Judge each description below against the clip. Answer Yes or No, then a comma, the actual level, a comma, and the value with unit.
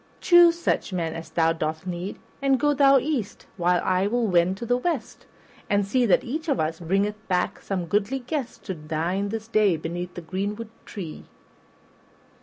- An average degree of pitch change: No, wide, 5.8 semitones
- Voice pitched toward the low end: No, high, 200 Hz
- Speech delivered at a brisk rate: No, average, 180 wpm